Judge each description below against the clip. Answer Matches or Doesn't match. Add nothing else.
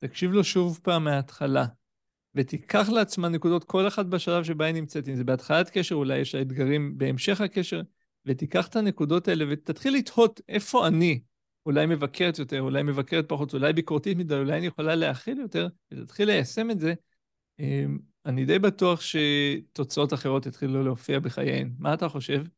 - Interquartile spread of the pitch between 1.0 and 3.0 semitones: Doesn't match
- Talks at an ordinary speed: Doesn't match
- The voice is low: Doesn't match